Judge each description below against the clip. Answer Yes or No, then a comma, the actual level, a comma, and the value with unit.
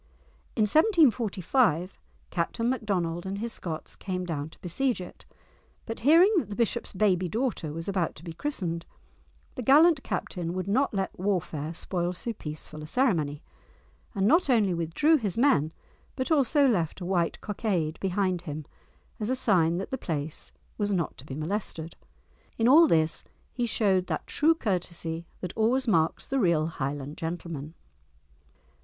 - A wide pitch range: Yes, wide, 6.2 semitones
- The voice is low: No, medium, 185 Hz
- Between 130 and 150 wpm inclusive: No, average, 160 wpm